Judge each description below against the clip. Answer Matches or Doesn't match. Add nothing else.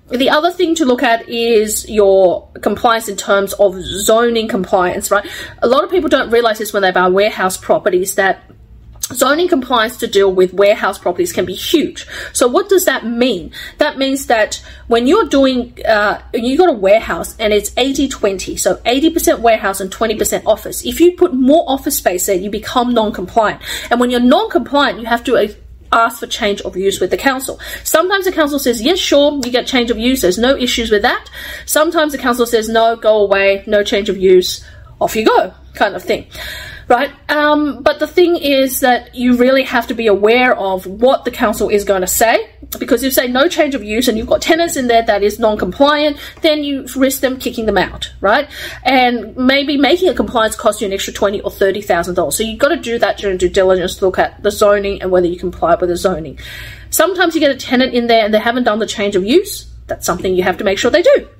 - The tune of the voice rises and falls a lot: Matches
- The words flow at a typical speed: Doesn't match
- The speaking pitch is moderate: Doesn't match